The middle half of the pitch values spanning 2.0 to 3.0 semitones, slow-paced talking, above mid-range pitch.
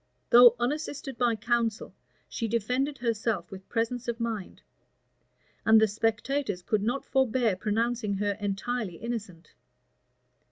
Yes: average, 2.7 semitones; slow, 120 wpm; high, 230 Hz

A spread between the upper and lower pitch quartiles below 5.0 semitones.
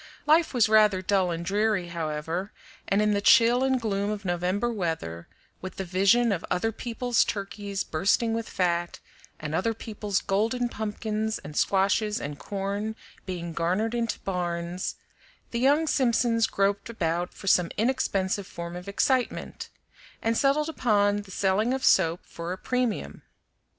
Yes: average, 4.2 semitones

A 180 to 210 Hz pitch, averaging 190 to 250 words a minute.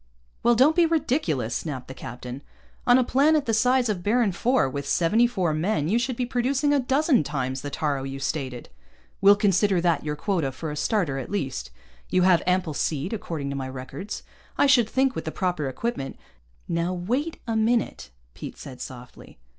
Yes: medium, 185 Hz; average, 195 wpm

